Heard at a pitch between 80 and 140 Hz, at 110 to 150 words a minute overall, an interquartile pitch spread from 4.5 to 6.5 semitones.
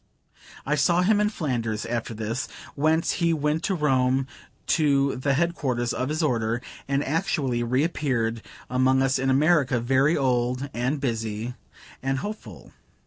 No: low, 135 Hz; average, 145 wpm; average, 3.9 semitones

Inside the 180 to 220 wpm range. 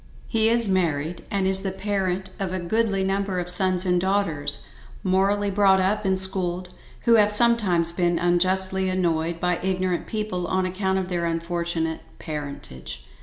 No: average, 160 wpm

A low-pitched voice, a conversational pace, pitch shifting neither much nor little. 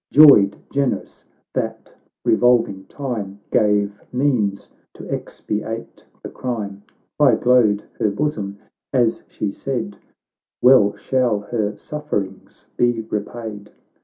No: low, 110 Hz; slow, 105 wpm; average, 3.5 semitones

